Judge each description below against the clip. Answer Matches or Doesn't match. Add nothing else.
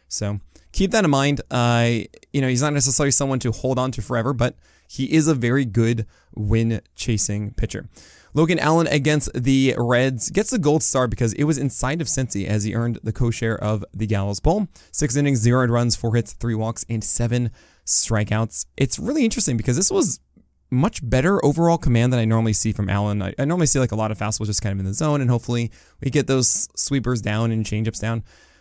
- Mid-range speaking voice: Doesn't match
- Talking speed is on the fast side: Matches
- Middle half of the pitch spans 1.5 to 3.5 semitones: Doesn't match